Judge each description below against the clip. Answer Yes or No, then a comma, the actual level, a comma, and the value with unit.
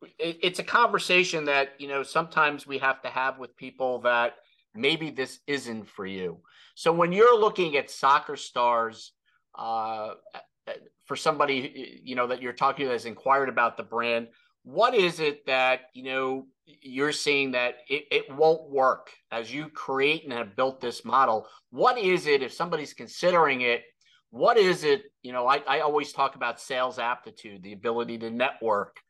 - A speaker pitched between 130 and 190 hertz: Yes, low, 135 Hz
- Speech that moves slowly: No, average, 175 wpm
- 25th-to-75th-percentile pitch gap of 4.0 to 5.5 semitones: Yes, average, 4.5 semitones